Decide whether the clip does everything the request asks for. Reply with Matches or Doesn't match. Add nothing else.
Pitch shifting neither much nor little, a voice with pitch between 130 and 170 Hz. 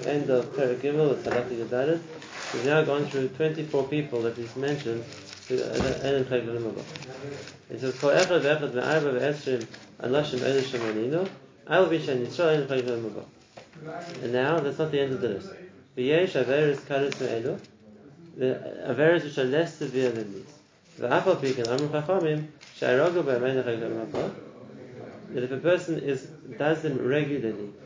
Matches